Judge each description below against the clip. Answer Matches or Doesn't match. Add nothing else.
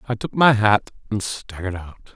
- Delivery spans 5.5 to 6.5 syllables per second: Doesn't match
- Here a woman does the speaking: Doesn't match